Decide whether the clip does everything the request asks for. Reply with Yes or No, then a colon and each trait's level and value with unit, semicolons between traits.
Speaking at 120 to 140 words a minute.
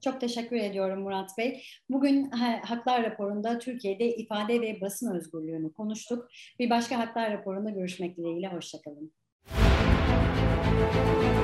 No: average, 110 wpm